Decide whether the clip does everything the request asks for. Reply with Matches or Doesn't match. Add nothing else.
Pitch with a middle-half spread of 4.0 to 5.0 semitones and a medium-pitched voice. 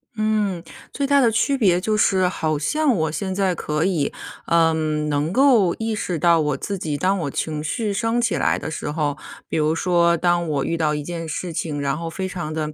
Matches